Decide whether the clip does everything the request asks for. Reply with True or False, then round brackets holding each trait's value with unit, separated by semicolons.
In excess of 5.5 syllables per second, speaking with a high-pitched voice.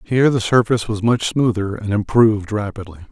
False (5.8 syllables/s; 110 Hz)